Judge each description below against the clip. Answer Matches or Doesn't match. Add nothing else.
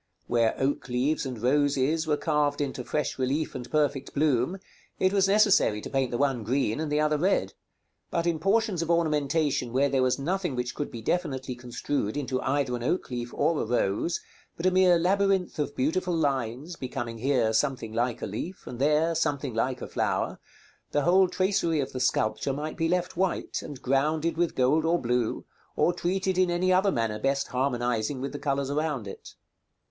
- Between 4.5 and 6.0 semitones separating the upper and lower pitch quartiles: Matches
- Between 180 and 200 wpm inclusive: Matches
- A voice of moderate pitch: Matches